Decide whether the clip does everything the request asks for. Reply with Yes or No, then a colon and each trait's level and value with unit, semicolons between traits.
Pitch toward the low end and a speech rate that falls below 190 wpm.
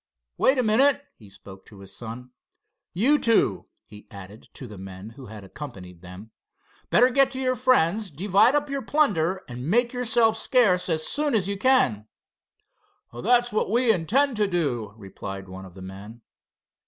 No: medium, 175 Hz; average, 170 wpm